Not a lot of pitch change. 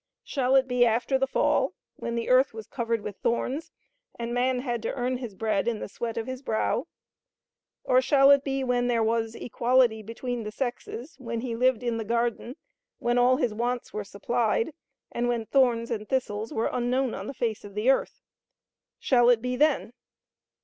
Yes: narrow, 2.1 semitones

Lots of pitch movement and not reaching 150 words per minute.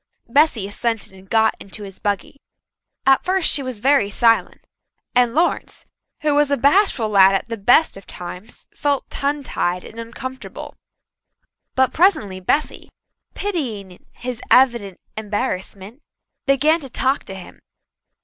Yes: wide, 5.9 semitones; average, 140 wpm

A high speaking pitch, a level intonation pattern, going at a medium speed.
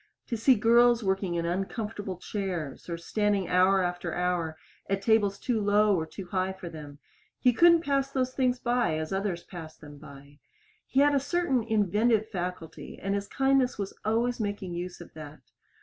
No: high, 200 Hz; average, 5.1 semitones; average, 180 wpm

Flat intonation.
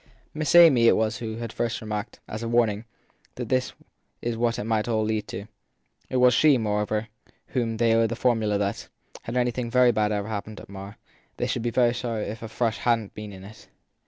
Yes: narrow, 2.0 semitones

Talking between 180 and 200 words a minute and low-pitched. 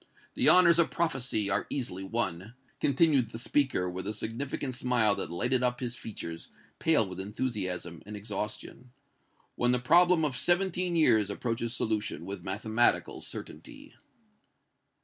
No: average, 140 wpm; low, 120 Hz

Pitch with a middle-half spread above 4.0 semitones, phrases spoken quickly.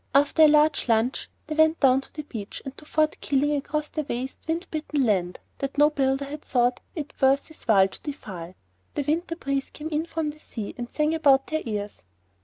No: average, 3.3 semitones; fast, 210 wpm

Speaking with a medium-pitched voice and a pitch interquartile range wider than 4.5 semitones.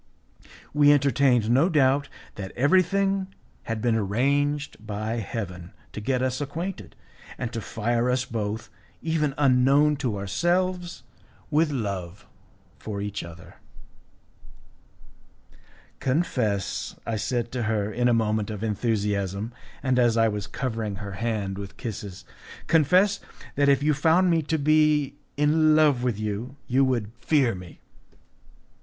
No: low, 125 Hz; wide, 5.6 semitones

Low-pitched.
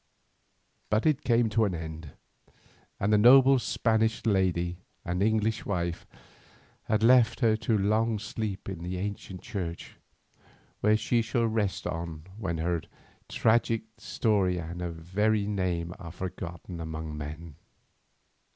Yes: low, 100 Hz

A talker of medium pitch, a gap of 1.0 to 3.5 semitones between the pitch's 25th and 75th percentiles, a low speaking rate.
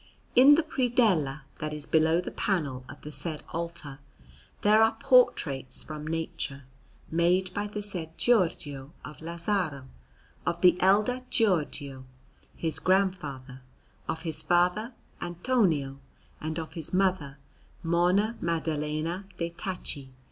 No: medium, 170 Hz; average, 4.3 semitones; slow, 125 wpm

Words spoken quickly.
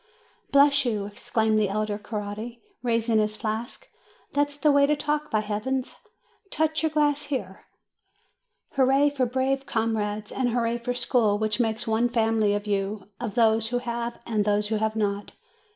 No: average, 165 wpm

